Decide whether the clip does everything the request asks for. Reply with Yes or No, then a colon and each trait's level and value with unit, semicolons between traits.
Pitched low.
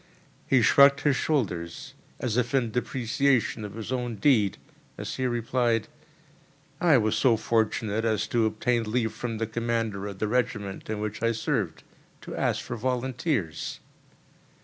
Yes: low, 115 Hz